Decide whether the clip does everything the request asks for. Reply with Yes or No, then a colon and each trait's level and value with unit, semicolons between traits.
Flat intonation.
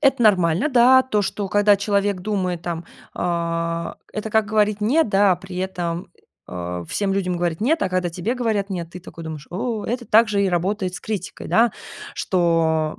No: average, 3.7 semitones